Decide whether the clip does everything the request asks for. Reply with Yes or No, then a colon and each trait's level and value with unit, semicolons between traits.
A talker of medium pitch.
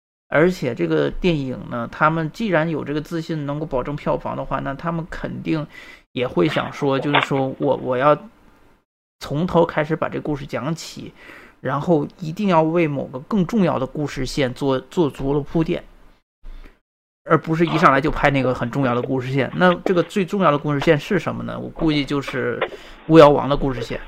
Yes: medium, 150 Hz